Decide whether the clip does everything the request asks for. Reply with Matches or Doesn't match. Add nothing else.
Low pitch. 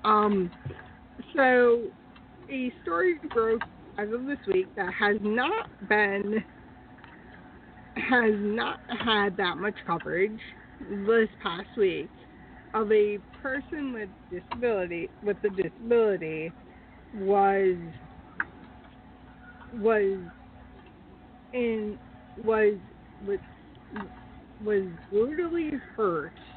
Doesn't match